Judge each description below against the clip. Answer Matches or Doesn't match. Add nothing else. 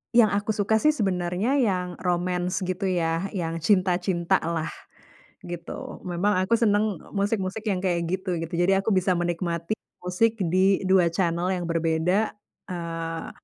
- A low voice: Doesn't match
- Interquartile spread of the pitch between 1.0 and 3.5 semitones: Matches